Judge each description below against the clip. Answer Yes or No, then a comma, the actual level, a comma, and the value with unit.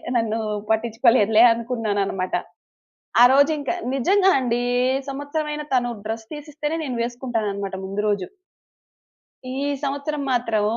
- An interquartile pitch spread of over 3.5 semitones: Yes, average, 4.4 semitones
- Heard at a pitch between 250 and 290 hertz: No, high, 240 Hz